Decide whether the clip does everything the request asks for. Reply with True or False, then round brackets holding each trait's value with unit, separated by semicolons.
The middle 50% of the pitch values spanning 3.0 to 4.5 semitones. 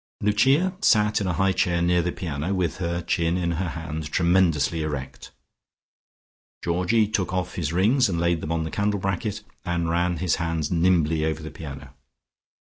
False (2.5 semitones)